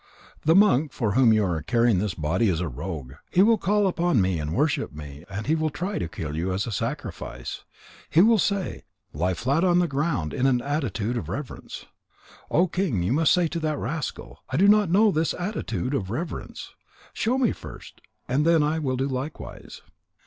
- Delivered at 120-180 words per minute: No, average, 200 wpm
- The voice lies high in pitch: No, low, 135 Hz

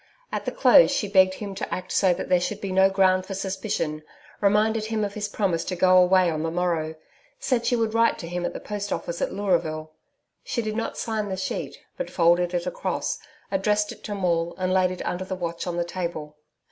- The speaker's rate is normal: No, fast, 225 wpm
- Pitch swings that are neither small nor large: Yes, average, 3.0 semitones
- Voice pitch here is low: No, medium, 185 Hz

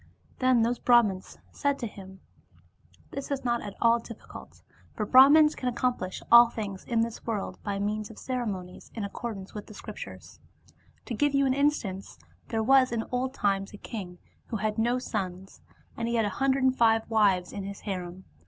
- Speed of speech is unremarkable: Yes, average, 195 wpm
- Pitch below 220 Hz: No, high, 225 Hz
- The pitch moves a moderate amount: Yes, average, 4.0 semitones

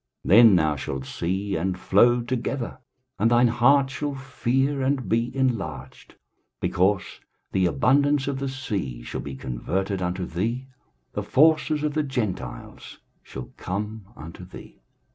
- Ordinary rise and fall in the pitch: No, wide, 6.6 semitones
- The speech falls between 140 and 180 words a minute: Yes, average, 145 wpm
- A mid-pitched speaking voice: No, low, 115 Hz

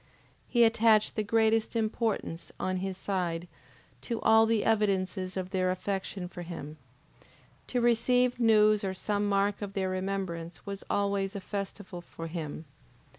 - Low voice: No, high, 200 Hz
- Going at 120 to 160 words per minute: Yes, average, 145 wpm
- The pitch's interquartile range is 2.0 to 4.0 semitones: Yes, average, 2.9 semitones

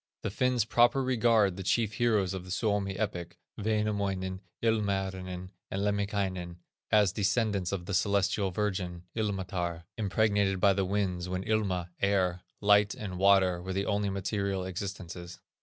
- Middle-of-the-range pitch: No, low, 100 Hz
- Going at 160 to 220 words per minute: No, average, 140 wpm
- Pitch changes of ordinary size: No, narrow, 2.1 semitones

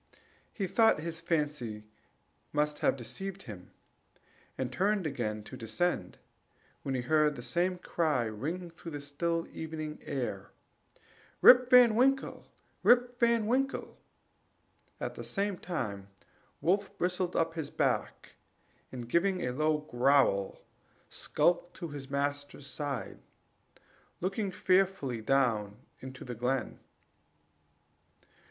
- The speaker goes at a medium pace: No, slow, 120 wpm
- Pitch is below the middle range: No, medium, 155 Hz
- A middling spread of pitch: No, wide, 6.3 semitones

